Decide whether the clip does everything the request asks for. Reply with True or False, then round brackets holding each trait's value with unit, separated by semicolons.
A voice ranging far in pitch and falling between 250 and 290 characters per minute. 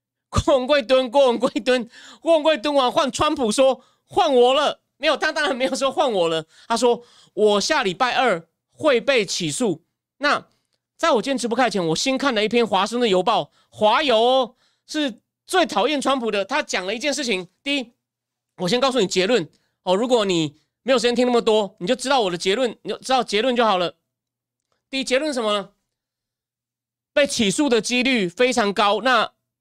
False (5.0 semitones; 270 characters per minute)